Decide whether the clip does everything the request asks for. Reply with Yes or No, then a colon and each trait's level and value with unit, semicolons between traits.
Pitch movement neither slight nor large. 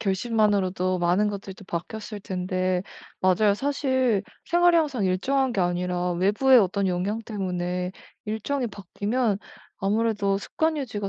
Yes: average, 3.9 semitones